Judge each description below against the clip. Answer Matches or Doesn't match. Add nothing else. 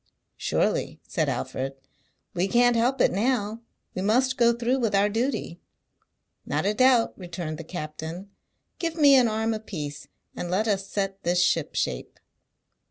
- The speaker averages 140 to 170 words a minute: Matches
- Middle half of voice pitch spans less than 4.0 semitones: Doesn't match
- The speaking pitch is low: Doesn't match